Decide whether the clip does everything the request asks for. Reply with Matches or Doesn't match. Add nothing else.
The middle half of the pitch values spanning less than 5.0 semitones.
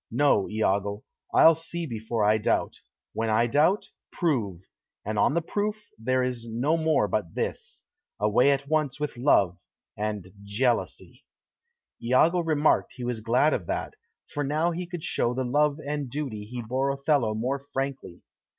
Doesn't match